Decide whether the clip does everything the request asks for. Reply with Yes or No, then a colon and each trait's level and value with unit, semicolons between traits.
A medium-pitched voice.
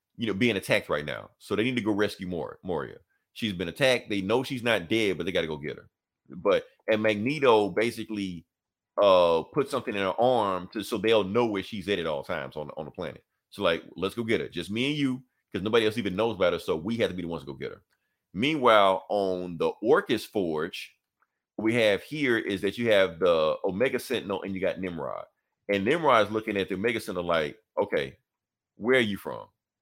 No: low, 105 Hz